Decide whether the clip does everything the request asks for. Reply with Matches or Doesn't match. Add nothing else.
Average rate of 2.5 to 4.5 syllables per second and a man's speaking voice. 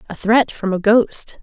Doesn't match